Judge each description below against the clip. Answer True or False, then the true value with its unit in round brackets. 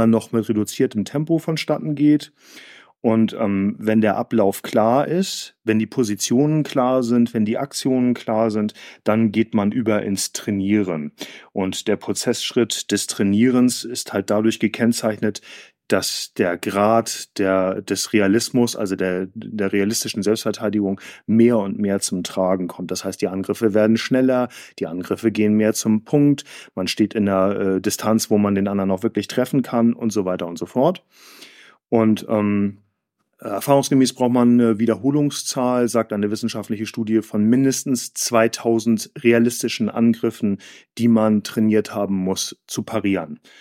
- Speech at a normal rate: True (150 wpm)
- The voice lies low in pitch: True (110 Hz)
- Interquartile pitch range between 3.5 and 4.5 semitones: False (2.8 semitones)